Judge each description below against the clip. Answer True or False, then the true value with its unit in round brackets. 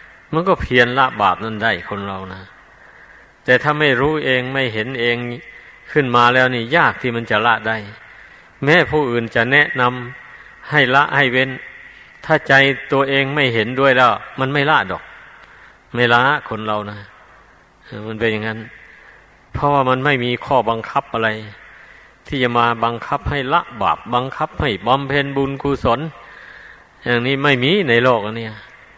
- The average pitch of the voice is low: True (125 Hz)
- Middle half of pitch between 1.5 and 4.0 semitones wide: True (3.6 semitones)